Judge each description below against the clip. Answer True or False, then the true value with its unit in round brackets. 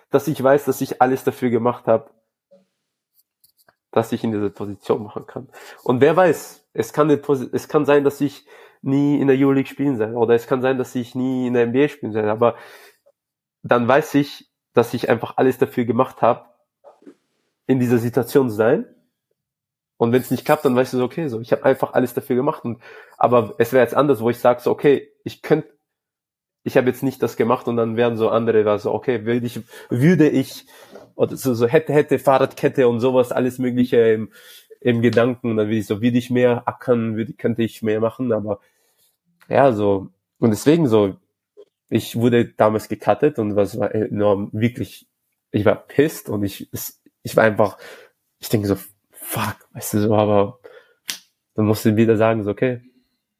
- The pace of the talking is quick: True (195 wpm)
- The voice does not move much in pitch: False (3.4 semitones)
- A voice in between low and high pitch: False (125 Hz)